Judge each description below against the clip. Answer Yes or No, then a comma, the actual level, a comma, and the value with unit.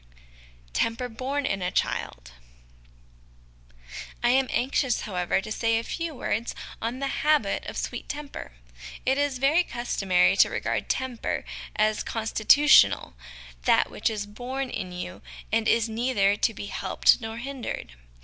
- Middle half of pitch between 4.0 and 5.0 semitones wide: Yes, average, 4.3 semitones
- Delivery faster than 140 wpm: Yes, average, 150 wpm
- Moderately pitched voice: No, high, 230 Hz